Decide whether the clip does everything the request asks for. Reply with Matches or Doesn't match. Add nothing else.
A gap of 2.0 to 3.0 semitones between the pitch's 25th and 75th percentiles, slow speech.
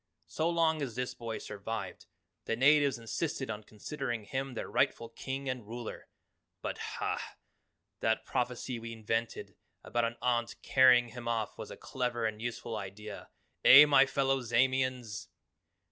Doesn't match